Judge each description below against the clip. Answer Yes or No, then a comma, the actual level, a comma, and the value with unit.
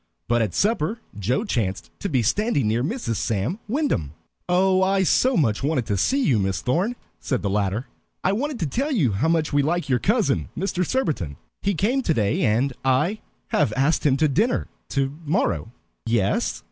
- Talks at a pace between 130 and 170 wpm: No, average, 185 wpm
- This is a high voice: No, medium, 145 Hz